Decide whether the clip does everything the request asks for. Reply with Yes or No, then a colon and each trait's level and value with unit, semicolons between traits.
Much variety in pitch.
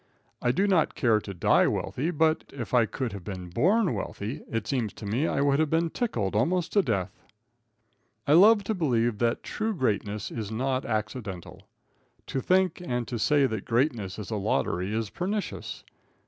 Yes: wide, 7.2 semitones